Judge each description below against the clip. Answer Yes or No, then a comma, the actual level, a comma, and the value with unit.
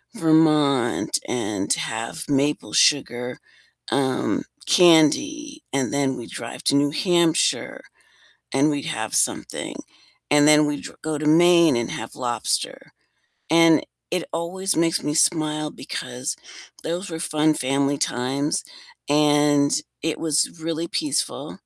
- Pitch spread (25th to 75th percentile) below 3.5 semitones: Yes, average, 3.1 semitones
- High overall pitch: No, medium, 150 Hz